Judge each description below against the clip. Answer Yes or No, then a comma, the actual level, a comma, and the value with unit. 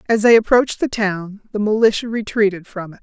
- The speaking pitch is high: Yes, high, 210 Hz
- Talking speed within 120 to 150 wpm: No, average, 200 wpm